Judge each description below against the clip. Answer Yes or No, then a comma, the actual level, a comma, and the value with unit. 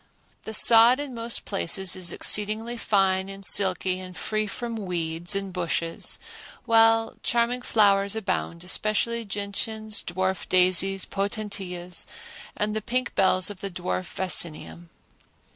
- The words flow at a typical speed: No, slow, 125 wpm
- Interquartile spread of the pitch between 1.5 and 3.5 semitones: Yes, average, 3.2 semitones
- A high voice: Yes, high, 195 Hz